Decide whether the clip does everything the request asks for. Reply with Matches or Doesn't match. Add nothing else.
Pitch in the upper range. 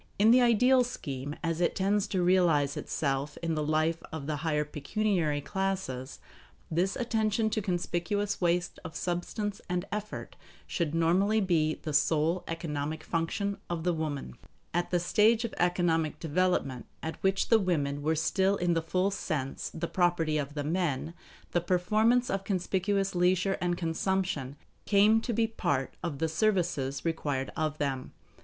Doesn't match